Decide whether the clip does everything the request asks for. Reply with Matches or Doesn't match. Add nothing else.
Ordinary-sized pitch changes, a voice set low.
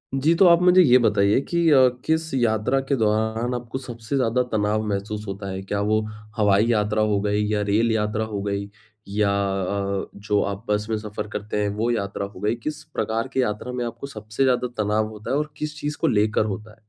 Matches